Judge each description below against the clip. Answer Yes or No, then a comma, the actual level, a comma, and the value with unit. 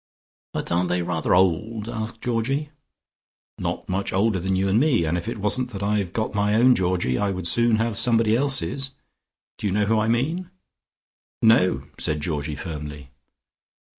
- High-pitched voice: No, low, 105 Hz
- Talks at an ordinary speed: Yes, average, 170 wpm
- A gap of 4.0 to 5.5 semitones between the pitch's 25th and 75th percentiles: Yes, average, 4.4 semitones